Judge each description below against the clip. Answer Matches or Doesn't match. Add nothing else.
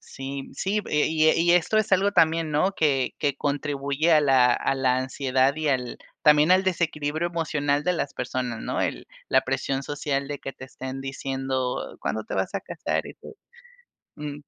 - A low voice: Doesn't match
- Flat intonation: Doesn't match